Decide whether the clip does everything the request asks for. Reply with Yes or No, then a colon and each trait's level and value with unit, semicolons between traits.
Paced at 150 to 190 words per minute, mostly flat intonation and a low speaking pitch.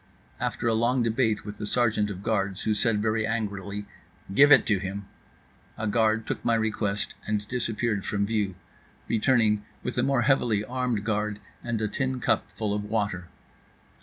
Yes: average, 170 wpm; narrow, 2.1 semitones; low, 110 Hz